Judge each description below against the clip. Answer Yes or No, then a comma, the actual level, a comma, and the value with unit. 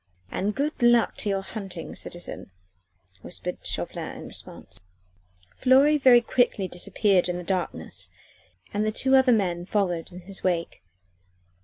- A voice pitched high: Yes, high, 200 Hz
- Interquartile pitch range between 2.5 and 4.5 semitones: No, average, 5.1 semitones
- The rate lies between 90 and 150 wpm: Yes, average, 140 wpm